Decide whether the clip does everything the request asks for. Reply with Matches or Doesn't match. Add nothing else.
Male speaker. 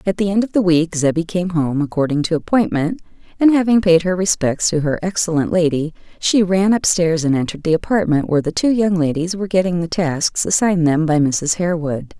Doesn't match